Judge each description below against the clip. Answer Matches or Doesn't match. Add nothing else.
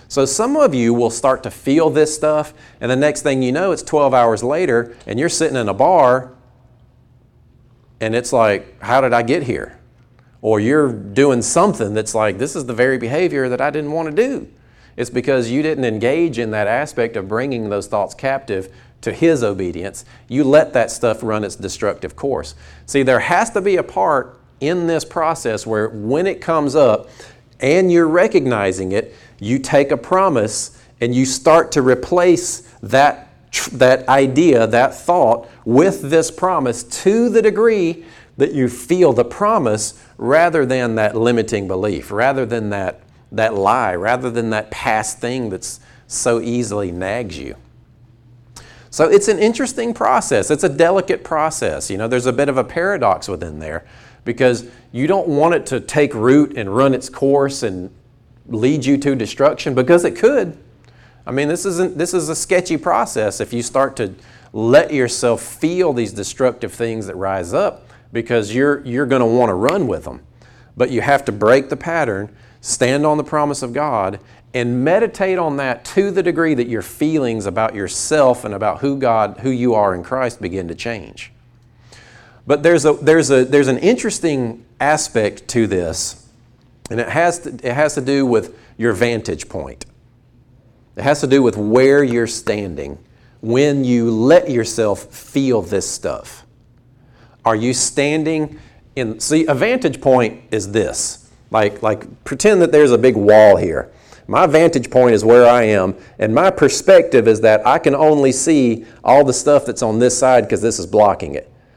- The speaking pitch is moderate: Doesn't match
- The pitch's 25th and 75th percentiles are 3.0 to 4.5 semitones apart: Matches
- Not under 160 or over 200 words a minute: Matches